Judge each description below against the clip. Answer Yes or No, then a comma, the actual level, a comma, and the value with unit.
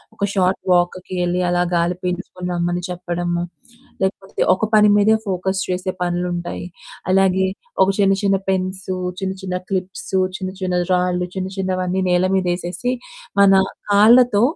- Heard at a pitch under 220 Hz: Yes, medium, 185 Hz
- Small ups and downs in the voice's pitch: Yes, narrow, 1.4 semitones